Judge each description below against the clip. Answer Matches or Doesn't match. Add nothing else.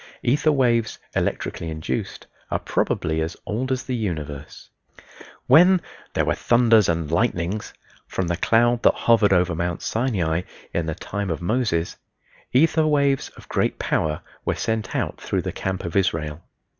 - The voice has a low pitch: Matches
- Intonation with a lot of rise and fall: Matches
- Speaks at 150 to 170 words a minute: Matches